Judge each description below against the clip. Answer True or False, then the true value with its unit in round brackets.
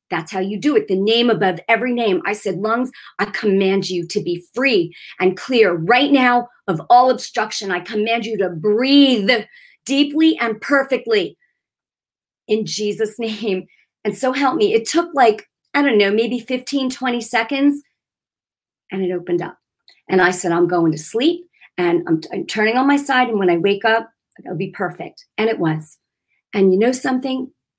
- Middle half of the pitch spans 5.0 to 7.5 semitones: True (5.4 semitones)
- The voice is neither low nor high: False (225 Hz)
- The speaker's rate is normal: True (185 wpm)